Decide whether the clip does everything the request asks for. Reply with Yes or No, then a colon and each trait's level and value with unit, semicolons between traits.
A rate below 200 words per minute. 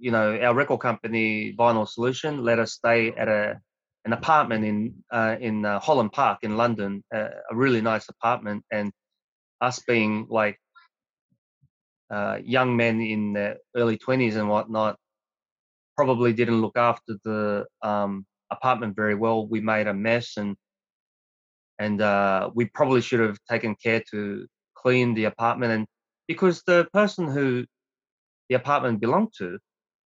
Yes: average, 150 wpm